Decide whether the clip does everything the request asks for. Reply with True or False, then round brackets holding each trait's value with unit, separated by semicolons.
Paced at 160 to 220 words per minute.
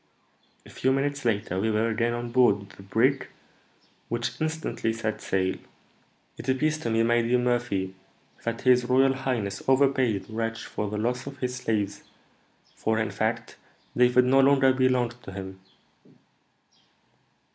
False (150 wpm)